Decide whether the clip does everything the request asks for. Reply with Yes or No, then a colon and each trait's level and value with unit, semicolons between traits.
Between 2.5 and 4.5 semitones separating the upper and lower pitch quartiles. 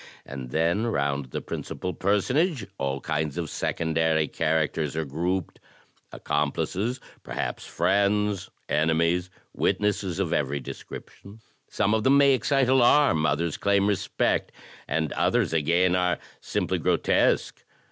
No: average, 5.0 semitones